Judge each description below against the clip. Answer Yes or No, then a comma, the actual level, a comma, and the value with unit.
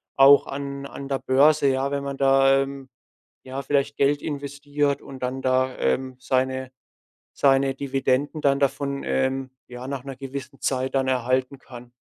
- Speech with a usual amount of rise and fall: No, narrow, 1.1 semitones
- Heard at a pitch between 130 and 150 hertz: Yes, low, 135 Hz